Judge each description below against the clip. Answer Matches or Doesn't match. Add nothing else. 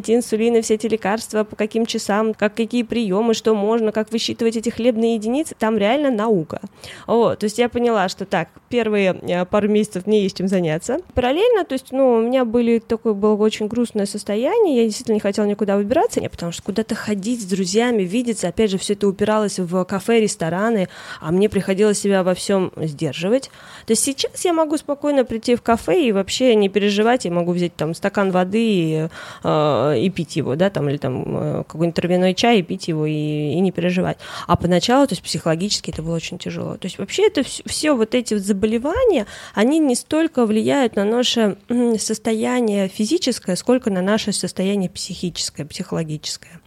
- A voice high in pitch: Matches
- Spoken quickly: Matches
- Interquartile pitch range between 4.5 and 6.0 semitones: Doesn't match